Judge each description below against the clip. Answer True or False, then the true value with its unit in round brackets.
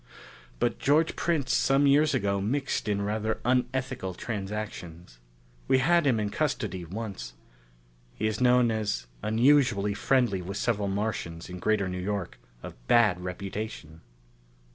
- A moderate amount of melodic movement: True (4.8 semitones)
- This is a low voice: True (105 Hz)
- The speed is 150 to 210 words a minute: False (135 wpm)